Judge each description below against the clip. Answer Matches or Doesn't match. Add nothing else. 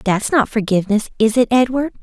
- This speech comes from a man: Doesn't match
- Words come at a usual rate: Matches